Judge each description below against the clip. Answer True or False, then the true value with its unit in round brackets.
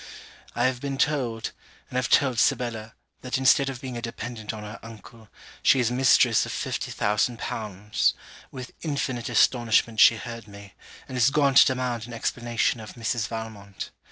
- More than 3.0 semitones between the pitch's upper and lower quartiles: False (2.4 semitones)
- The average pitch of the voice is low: True (120 Hz)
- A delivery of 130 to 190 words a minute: True (170 wpm)